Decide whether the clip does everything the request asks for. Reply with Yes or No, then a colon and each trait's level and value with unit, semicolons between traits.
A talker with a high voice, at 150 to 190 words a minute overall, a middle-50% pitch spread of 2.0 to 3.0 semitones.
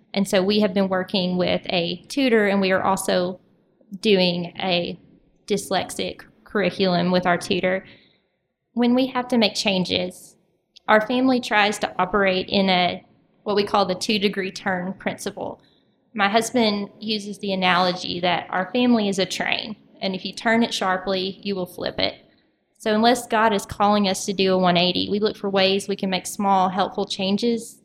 Yes: high, 195 Hz; average, 175 wpm; narrow, 2.5 semitones